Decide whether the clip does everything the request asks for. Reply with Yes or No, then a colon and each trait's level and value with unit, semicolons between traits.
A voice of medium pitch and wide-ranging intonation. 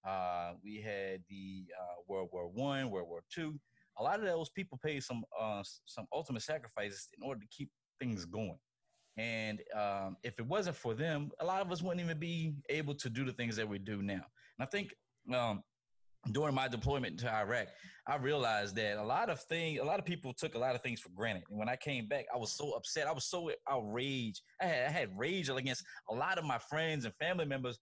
No: low, 120 Hz; wide, 6.5 semitones